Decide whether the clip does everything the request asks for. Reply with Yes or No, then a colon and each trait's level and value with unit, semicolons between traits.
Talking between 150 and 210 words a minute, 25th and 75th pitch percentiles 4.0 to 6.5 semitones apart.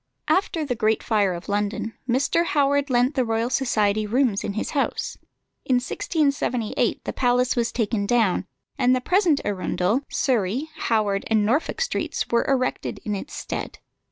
Yes: average, 155 wpm; average, 4.5 semitones